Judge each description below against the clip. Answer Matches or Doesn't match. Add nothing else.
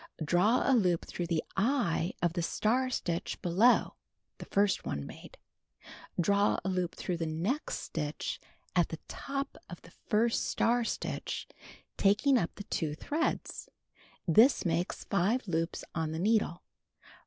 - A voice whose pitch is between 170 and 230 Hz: Matches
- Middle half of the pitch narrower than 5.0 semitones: Doesn't match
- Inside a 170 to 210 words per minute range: Doesn't match